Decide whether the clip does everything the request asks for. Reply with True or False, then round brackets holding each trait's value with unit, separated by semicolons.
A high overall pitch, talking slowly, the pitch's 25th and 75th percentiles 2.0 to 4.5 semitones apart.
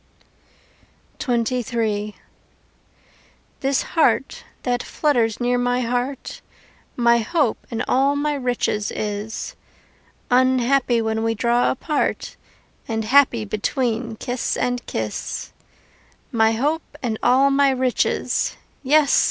True (245 Hz; 105 wpm; 3.1 semitones)